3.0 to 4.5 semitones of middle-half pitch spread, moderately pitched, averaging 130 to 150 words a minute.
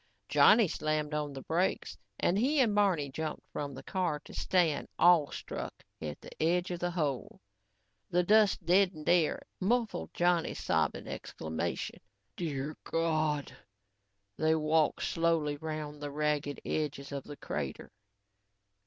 Yes: average, 3.3 semitones; medium, 155 Hz; slow, 135 wpm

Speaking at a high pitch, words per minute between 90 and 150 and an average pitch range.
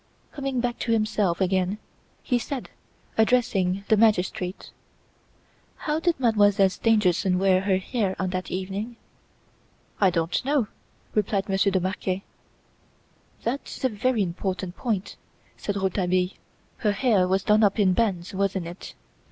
Yes: high, 200 Hz; slow, 135 wpm; average, 3.3 semitones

